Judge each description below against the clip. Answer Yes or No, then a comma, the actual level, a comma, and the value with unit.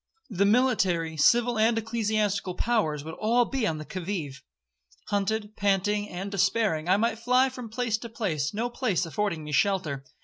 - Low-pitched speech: No, high, 205 Hz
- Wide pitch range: No, average, 4.4 semitones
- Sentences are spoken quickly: No, average, 165 wpm